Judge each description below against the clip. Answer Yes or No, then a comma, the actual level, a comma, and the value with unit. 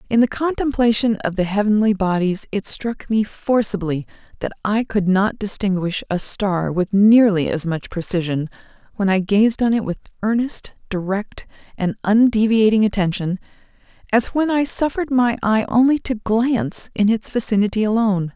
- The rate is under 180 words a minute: Yes, average, 155 wpm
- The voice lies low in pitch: No, high, 210 Hz